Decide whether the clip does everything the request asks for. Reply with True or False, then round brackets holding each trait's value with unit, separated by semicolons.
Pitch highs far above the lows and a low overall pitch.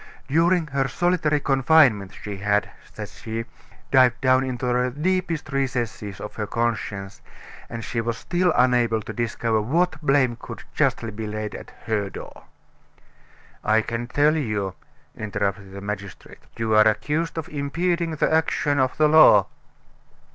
True (5.7 semitones; 125 Hz)